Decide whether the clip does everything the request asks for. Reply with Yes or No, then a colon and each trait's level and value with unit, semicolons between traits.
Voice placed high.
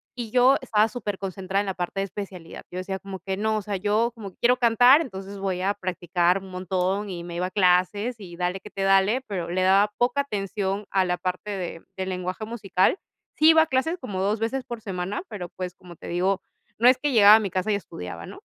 Yes: high, 195 Hz